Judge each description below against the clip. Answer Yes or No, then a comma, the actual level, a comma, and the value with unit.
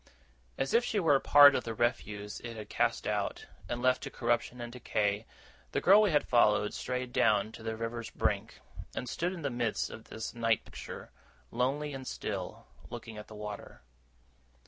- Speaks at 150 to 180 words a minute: No, average, 190 wpm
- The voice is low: Yes, low, 120 Hz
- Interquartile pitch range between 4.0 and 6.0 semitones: No, average, 3.5 semitones